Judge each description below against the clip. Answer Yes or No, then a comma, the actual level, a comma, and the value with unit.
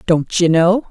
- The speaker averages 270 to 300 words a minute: No, average, 200 wpm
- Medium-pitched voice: Yes, medium, 180 Hz